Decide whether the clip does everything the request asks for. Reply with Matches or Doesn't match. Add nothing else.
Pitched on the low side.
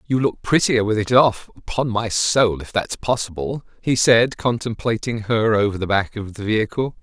Matches